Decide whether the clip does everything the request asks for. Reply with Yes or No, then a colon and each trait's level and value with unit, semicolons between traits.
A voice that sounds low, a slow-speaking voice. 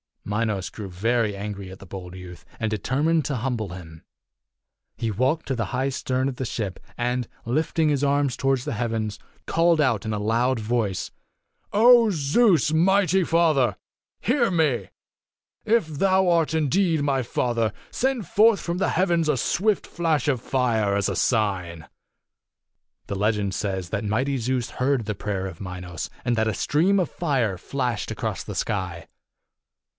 No: low, 125 Hz; average, 165 wpm